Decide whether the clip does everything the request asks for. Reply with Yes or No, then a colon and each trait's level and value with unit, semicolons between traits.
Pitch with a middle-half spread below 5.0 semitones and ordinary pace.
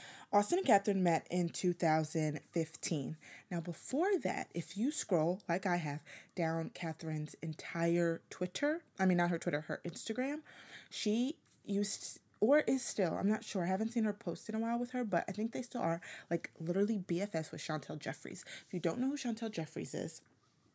No: average, 5.3 semitones; average, 185 wpm